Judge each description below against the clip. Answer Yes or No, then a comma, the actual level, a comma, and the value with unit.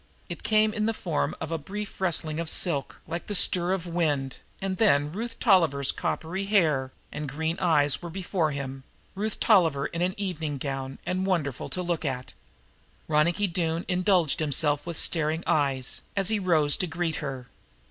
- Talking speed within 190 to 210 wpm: No, average, 180 wpm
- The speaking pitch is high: No, medium, 165 Hz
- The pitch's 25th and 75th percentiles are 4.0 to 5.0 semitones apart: Yes, average, 4.3 semitones